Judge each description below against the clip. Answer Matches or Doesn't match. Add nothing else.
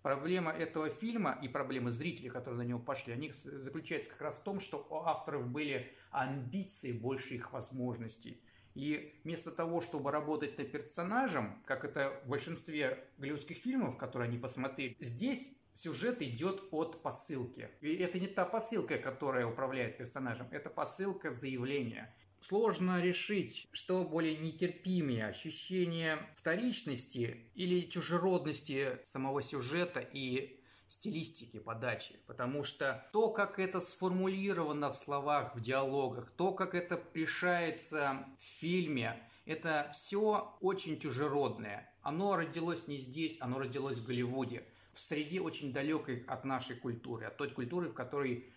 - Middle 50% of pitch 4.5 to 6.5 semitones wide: Matches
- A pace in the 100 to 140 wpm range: Matches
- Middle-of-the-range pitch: Matches